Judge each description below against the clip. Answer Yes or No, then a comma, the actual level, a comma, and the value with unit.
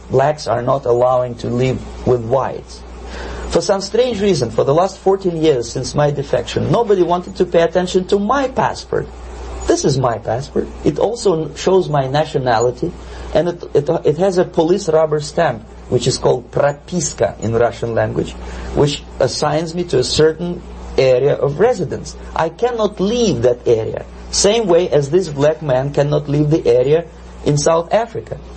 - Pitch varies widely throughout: Yes, wide, 6.7 semitones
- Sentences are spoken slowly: No, average, 170 wpm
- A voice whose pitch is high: No, medium, 150 Hz